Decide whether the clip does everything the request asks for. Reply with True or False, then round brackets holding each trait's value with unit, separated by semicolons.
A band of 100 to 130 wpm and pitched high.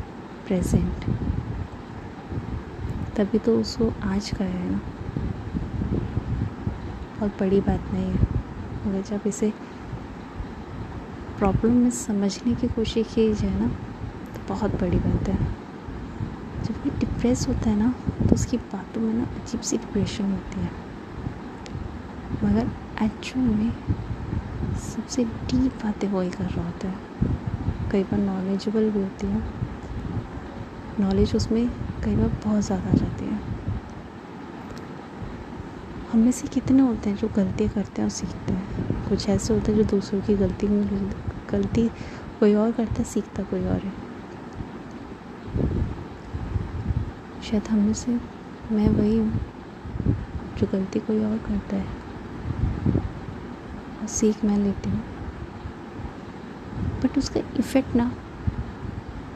True (125 wpm; 205 Hz)